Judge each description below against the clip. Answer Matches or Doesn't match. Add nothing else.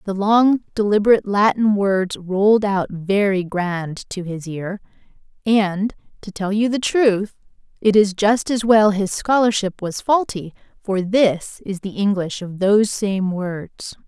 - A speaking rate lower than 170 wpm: Matches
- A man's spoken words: Doesn't match